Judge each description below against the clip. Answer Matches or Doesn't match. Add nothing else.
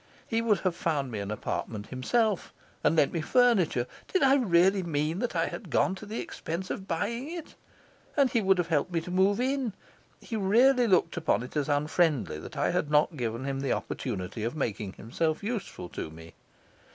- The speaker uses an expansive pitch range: Matches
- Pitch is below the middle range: Doesn't match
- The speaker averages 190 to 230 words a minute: Matches